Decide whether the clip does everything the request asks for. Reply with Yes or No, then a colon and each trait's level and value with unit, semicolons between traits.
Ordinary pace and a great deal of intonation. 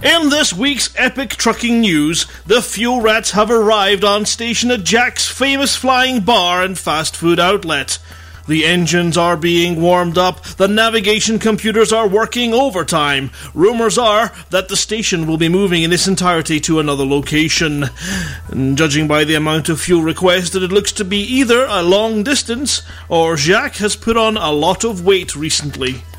Yes: average, 170 wpm; wide, 5.7 semitones